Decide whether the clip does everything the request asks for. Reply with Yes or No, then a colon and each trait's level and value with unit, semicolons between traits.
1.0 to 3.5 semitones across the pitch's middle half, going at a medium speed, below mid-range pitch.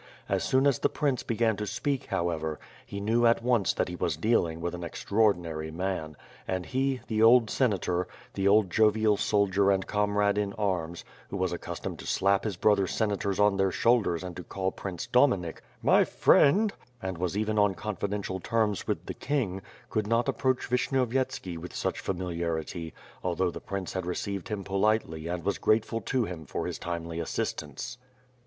No: average, 4.1 semitones; average, 175 wpm; low, 100 Hz